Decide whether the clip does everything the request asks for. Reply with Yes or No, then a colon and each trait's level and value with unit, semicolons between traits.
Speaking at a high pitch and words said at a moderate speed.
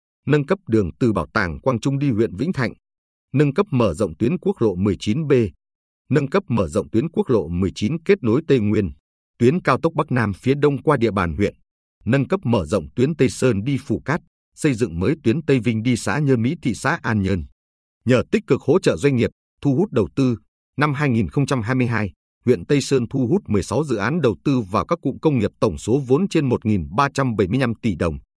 No: low, 125 Hz; average, 215 wpm